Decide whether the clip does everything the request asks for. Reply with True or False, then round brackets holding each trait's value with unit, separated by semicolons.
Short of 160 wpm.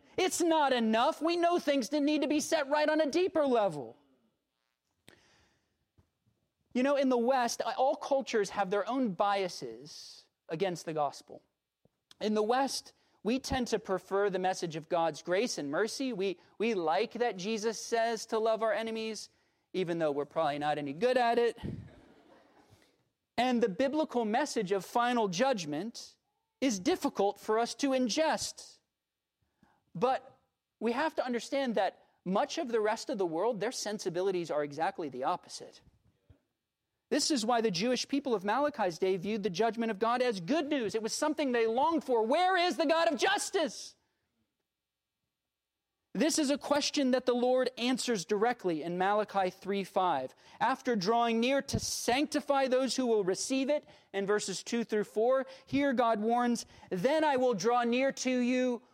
False (165 wpm)